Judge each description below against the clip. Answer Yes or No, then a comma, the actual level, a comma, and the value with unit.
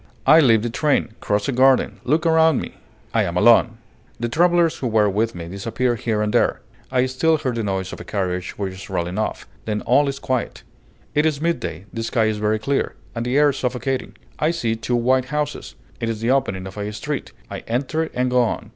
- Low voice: Yes, low, 120 Hz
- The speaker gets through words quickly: Yes, fast, 220 wpm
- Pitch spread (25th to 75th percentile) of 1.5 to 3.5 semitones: No, average, 4.4 semitones